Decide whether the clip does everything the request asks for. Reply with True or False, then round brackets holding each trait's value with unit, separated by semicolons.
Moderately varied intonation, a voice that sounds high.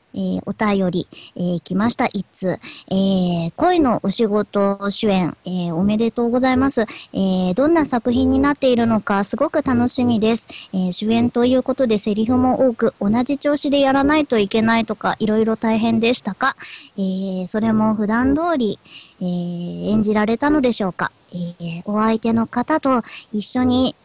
True (4.5 semitones; 225 Hz)